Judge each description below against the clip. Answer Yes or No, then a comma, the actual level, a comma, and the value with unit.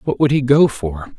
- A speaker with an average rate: No, fast, 255 wpm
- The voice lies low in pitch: Yes, low, 125 Hz